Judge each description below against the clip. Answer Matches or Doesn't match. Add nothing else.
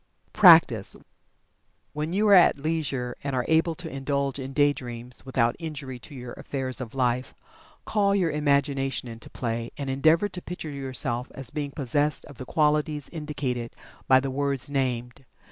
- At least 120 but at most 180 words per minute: Matches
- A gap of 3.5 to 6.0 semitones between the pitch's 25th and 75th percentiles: Doesn't match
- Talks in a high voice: Doesn't match